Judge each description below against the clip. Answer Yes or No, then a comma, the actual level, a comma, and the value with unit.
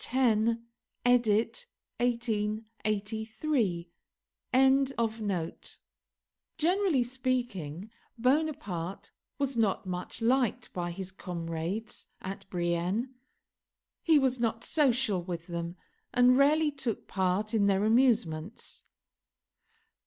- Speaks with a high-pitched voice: Yes, high, 220 Hz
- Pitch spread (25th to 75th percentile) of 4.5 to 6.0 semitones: Yes, average, 5.2 semitones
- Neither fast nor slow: No, slow, 85 wpm